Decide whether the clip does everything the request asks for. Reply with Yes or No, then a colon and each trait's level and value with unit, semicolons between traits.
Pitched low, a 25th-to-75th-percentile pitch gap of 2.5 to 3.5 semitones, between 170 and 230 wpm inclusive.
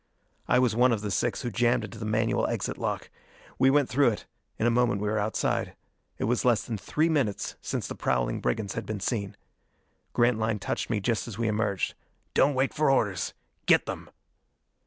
Yes: low, 115 Hz; average, 2.9 semitones; average, 200 wpm